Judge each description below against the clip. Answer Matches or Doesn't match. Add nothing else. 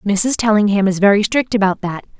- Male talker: Doesn't match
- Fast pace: Doesn't match